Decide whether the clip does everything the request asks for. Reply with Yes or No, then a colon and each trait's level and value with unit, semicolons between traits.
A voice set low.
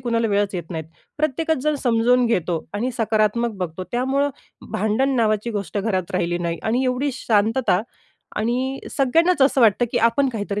No: high, 230 Hz